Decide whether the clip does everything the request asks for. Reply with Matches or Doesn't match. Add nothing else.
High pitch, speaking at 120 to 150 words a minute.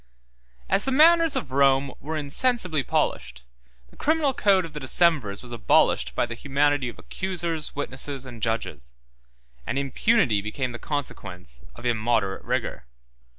Doesn't match